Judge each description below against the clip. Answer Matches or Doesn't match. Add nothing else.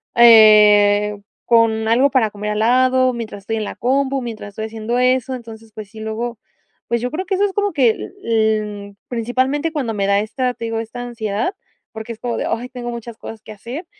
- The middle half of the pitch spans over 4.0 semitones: Doesn't match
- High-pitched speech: Matches